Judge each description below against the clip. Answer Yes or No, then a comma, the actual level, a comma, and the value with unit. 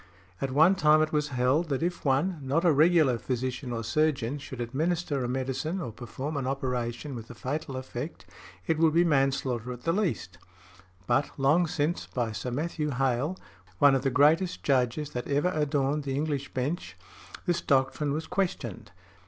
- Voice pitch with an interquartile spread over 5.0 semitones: No, average, 3.7 semitones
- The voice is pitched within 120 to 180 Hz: Yes, medium, 140 Hz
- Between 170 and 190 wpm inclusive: Yes, average, 175 wpm